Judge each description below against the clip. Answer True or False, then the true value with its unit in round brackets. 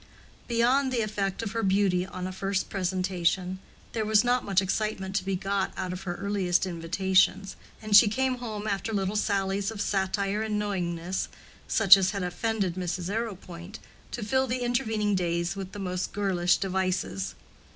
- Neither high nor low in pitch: False (195 Hz)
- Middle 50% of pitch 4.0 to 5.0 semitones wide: False (2.5 semitones)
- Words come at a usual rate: True (170 wpm)